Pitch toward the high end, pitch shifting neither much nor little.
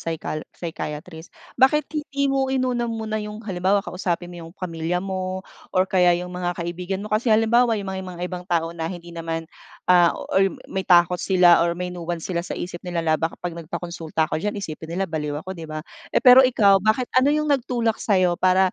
No: medium, 180 Hz; average, 3.8 semitones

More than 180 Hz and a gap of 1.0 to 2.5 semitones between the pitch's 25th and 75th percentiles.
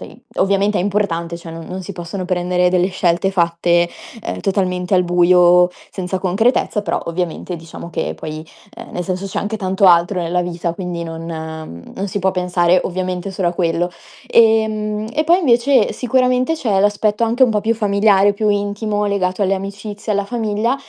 No: high, 190 Hz; average, 2.9 semitones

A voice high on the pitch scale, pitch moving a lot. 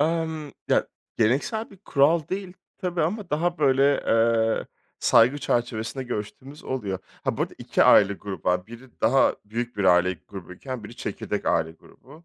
No: low, 130 Hz; wide, 6.4 semitones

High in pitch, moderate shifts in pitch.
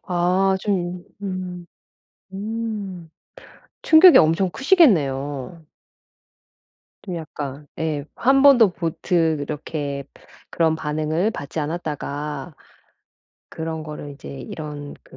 No: medium, 165 Hz; average, 4.2 semitones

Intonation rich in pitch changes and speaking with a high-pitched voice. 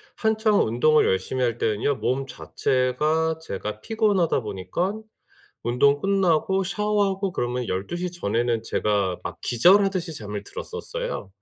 No: wide, 8.9 semitones; medium, 150 Hz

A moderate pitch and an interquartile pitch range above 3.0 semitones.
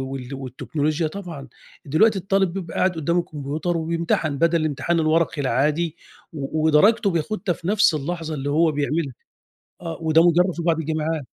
No: medium, 160 Hz; narrow, 2.6 semitones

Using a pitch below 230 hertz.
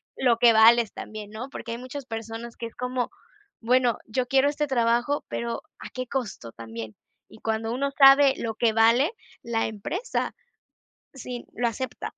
No: high, 235 Hz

